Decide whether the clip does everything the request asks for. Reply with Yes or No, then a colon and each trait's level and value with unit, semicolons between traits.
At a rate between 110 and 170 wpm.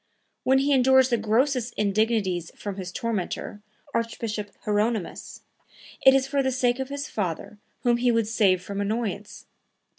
Yes: average, 150 wpm